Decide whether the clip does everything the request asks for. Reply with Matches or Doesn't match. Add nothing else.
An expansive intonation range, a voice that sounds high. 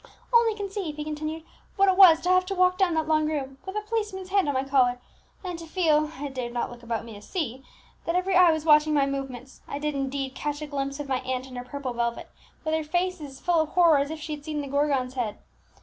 Doesn't match